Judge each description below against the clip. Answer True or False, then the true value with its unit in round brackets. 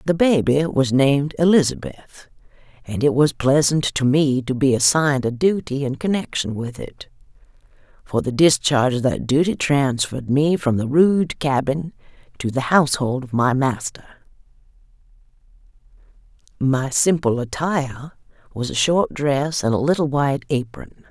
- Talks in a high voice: False (140 Hz)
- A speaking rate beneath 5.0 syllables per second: True (4.7 syllables/s)